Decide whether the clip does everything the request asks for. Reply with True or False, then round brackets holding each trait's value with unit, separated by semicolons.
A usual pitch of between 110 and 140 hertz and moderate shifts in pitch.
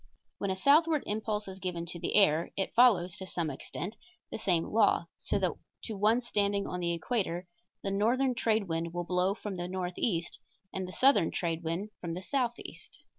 False (190 Hz; 3.8 semitones)